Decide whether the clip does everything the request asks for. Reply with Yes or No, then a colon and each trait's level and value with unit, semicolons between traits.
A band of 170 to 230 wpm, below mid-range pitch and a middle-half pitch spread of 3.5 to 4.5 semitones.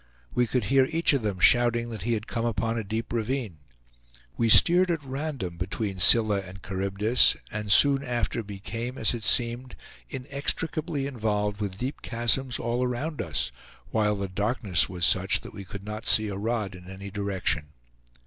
Yes: average, 175 wpm; low, 110 Hz; average, 4.1 semitones